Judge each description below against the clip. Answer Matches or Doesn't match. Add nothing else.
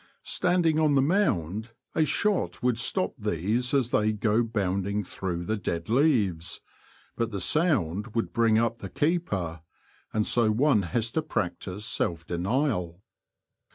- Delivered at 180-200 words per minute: Doesn't match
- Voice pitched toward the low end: Matches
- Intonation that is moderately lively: Doesn't match